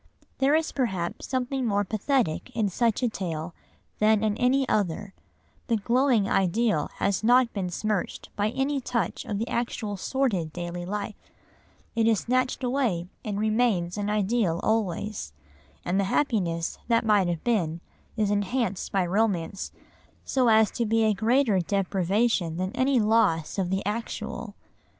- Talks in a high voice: Yes, high, 210 Hz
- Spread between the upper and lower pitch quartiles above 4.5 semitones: No, average, 4.1 semitones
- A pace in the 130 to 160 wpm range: Yes, average, 150 wpm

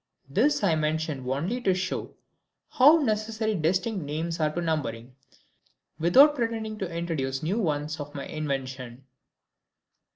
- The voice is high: No, medium, 165 Hz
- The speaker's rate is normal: No, slow, 130 wpm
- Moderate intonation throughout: No, wide, 6.8 semitones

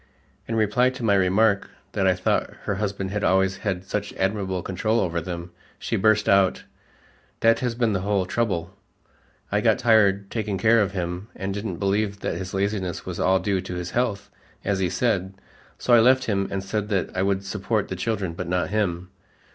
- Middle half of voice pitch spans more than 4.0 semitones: No, narrow, 2.4 semitones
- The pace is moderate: Yes, average, 195 wpm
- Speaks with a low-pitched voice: Yes, low, 100 Hz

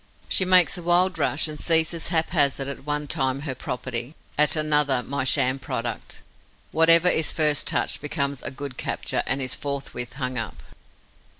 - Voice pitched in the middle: Yes, medium, 145 Hz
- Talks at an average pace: Yes, average, 165 wpm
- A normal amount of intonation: Yes, average, 3.5 semitones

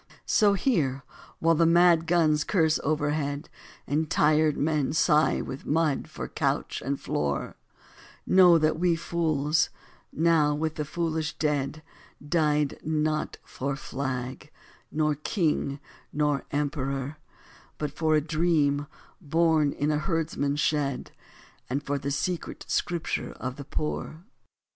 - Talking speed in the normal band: No, slow, 125 wpm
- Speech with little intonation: Yes, narrow, 2.2 semitones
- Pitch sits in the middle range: Yes, medium, 150 Hz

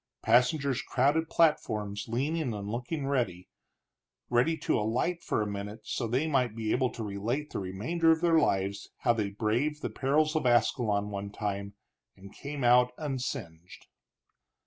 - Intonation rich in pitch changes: Yes, wide, 5.8 semitones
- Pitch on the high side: No, low, 120 Hz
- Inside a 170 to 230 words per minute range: No, average, 150 wpm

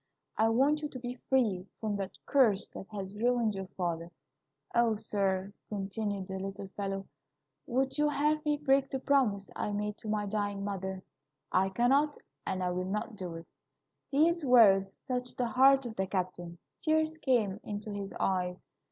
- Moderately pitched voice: No, high, 210 Hz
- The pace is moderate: Yes, average, 170 wpm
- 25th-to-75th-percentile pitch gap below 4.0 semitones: No, average, 5.0 semitones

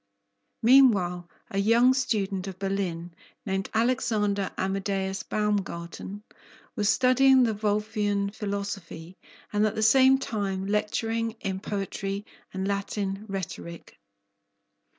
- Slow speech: Yes, slow, 105 wpm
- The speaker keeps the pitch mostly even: Yes, narrow, 2.2 semitones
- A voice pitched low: No, high, 200 Hz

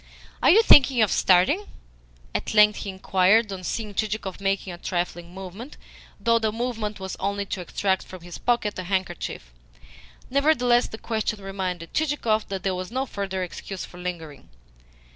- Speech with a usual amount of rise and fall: Yes, average, 3.5 semitones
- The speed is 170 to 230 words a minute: No, average, 160 wpm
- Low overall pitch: No, high, 200 Hz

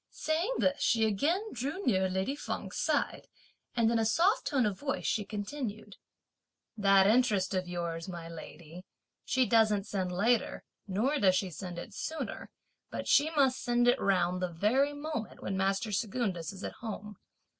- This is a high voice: Yes, high, 210 Hz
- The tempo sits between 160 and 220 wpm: Yes, average, 165 wpm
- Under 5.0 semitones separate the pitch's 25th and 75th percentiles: No, wide, 5.6 semitones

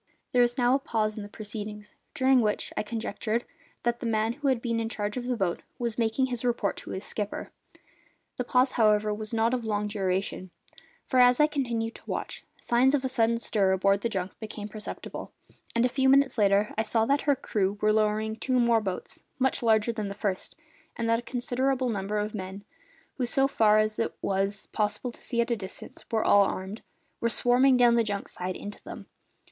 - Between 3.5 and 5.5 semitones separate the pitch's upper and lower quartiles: No, average, 2.8 semitones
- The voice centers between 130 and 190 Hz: No, high, 225 Hz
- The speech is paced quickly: Yes, fast, 210 wpm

